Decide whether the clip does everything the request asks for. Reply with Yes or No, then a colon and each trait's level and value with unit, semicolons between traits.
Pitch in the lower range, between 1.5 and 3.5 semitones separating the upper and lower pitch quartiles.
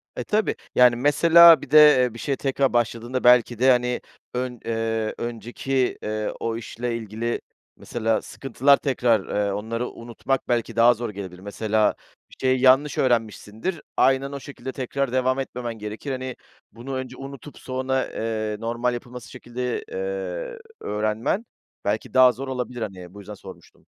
Yes: low, 125 Hz; average, 3.0 semitones